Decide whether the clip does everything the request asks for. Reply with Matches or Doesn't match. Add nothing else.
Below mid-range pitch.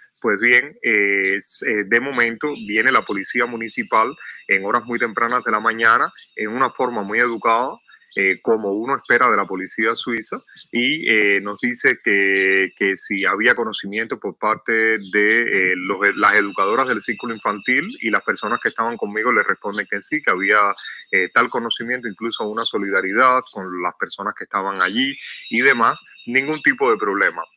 Matches